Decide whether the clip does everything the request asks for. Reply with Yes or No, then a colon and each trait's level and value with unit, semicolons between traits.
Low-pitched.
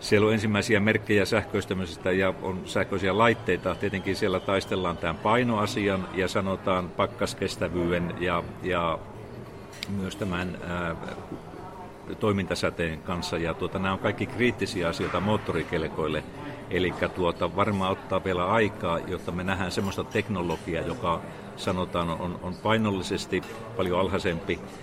Yes: very low, 95 Hz